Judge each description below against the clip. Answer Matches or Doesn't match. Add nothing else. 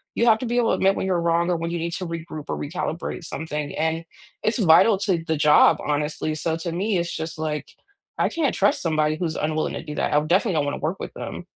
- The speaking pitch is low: Doesn't match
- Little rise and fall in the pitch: Doesn't match